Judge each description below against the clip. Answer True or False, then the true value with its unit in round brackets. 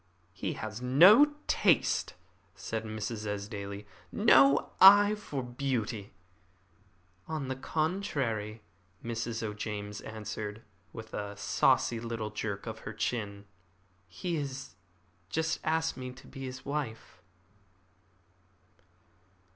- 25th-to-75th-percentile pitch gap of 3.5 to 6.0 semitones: True (4.7 semitones)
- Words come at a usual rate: False (105 wpm)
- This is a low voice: True (115 Hz)